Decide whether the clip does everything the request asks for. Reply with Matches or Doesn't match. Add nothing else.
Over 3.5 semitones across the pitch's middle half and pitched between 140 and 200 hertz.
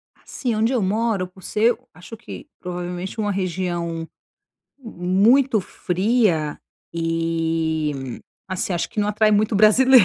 Matches